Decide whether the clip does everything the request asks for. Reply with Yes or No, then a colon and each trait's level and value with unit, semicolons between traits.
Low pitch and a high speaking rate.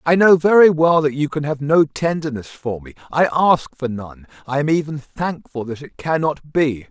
No: medium, 145 Hz; fast, 210 wpm